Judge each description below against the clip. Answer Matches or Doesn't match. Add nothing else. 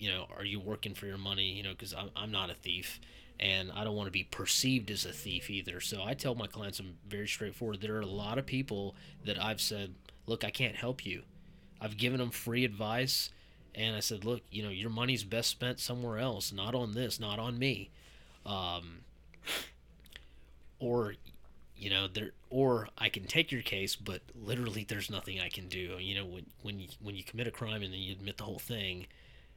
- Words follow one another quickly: Matches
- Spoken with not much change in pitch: Doesn't match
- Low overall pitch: Matches